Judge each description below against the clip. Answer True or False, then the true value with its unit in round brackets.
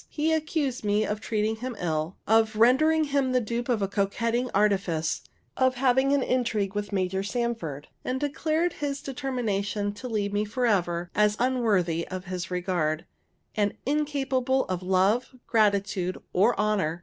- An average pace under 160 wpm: True (150 wpm)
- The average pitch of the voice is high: True (215 Hz)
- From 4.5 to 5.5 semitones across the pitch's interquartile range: True (4.9 semitones)